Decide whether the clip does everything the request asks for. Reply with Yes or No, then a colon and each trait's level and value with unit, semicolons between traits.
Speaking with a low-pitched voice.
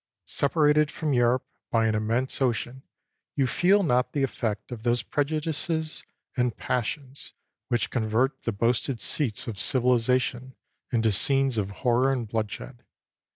Yes: low, 125 Hz